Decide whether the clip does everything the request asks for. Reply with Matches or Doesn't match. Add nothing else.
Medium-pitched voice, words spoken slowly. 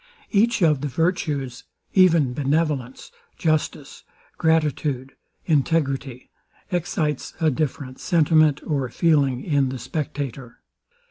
Matches